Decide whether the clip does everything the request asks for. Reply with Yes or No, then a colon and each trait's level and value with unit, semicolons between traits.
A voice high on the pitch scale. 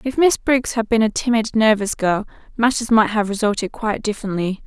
Yes: high, 220 Hz